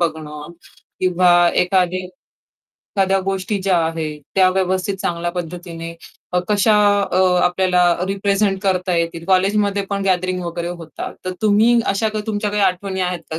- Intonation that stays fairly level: Yes, narrow, 2.2 semitones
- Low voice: No, medium, 185 Hz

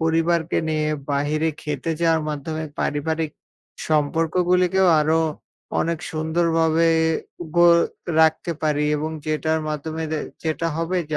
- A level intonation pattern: Yes, narrow, 1.3 semitones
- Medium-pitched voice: Yes, medium, 160 Hz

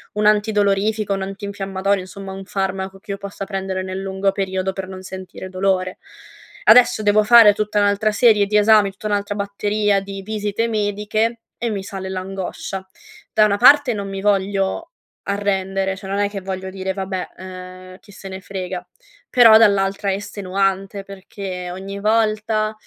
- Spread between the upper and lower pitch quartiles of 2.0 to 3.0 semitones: No, narrow, 1.6 semitones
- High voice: Yes, high, 195 Hz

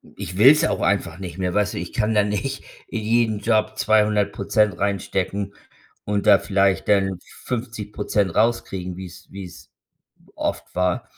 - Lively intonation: No, narrow, 2.4 semitones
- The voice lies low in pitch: Yes, low, 100 Hz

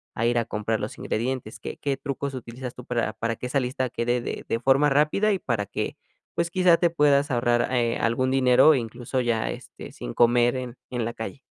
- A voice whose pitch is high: No, low, 125 Hz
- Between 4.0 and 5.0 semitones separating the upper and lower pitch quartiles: No, average, 2.7 semitones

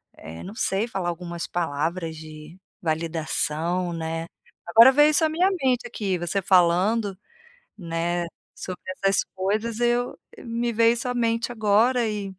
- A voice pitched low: No, high, 190 Hz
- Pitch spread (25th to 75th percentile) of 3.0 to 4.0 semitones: No, wide, 5.4 semitones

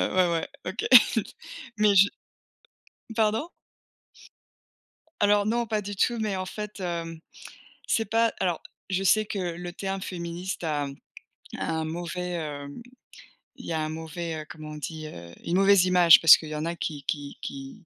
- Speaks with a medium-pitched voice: Yes, medium, 175 Hz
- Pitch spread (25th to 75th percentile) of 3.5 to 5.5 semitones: Yes, average, 4.1 semitones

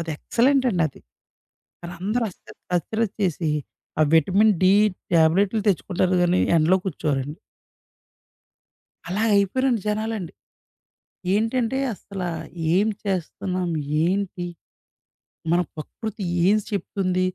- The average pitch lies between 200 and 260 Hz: No, high, 190 Hz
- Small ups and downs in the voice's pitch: No, average, 3.7 semitones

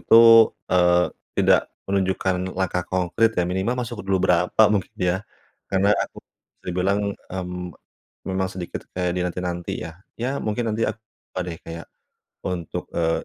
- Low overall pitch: Yes, very low, 90 Hz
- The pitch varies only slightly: Yes, narrow, 1.7 semitones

